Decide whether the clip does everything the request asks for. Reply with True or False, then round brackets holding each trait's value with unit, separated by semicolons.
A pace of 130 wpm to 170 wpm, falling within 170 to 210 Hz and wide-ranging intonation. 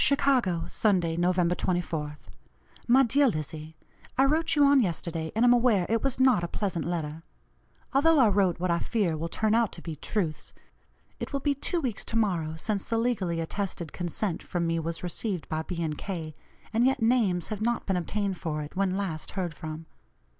False (195 wpm; 185 Hz; 5.8 semitones)